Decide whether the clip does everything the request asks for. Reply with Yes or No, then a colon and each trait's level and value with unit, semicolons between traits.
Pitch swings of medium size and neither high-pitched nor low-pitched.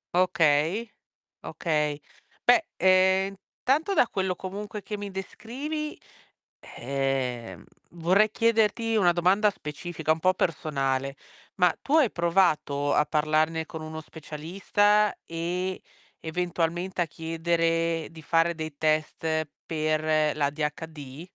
Yes: average, 3.7 semitones; medium, 165 Hz